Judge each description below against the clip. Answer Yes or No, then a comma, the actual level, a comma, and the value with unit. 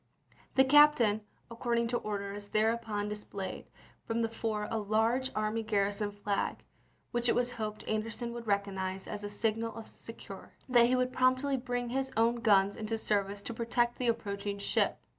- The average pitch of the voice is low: No, high, 225 Hz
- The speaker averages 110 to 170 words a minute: No, average, 180 wpm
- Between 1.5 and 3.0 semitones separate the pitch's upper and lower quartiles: Yes, average, 2.7 semitones